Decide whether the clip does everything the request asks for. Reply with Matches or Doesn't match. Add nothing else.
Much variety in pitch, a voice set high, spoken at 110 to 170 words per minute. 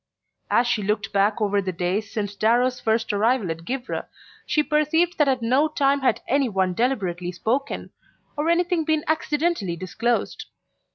Matches